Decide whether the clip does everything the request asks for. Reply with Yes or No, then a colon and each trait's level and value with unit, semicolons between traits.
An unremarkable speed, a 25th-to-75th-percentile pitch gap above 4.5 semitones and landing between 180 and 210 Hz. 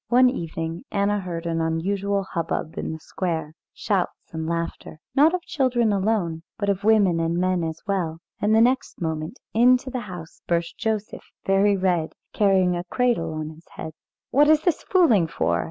Yes: average, 170 wpm; average, 5.1 semitones; high, 190 Hz